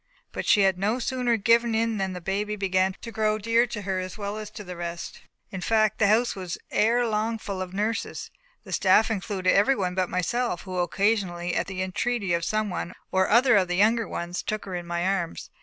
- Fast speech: Yes, fast, 225 wpm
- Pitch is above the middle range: Yes, high, 200 Hz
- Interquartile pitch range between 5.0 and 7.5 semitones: No, average, 3.2 semitones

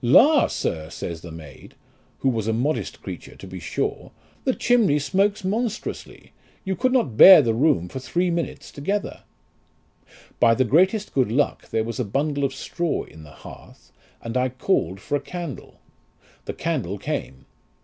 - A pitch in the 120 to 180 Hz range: Yes, medium, 140 Hz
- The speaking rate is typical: Yes, average, 170 wpm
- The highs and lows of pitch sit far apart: Yes, wide, 8.7 semitones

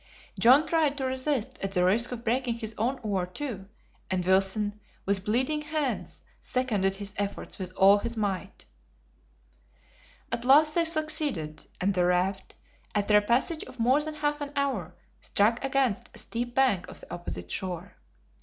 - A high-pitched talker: Yes, high, 230 Hz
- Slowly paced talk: No, average, 165 wpm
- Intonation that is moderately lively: No, wide, 5.9 semitones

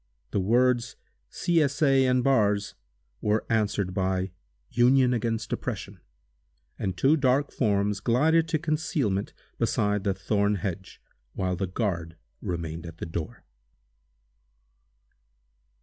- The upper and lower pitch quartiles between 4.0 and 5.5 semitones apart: Yes, average, 5.2 semitones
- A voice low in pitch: Yes, low, 105 Hz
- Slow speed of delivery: Yes, slow, 120 wpm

